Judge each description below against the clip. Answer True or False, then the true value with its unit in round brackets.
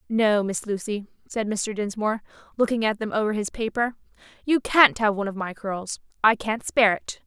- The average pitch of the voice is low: False (215 Hz)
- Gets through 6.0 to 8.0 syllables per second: False (5.4 syllables/s)